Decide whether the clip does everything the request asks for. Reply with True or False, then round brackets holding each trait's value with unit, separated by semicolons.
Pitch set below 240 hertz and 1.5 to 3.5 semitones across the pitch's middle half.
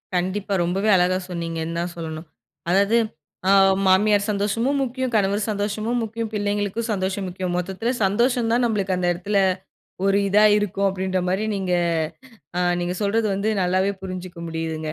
True (195 Hz; 2.8 semitones)